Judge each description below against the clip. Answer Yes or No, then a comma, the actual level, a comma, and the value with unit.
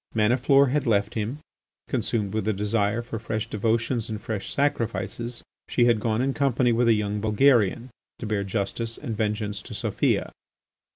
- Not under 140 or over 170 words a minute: Yes, average, 165 wpm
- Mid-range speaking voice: No, low, 115 Hz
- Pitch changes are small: Yes, narrow, 2.2 semitones